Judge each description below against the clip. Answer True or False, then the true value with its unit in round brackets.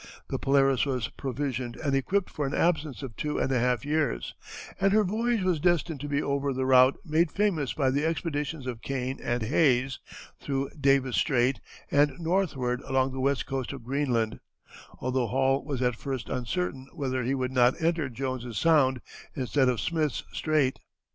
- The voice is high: False (135 Hz)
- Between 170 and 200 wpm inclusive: True (175 wpm)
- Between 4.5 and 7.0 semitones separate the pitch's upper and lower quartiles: False (3.0 semitones)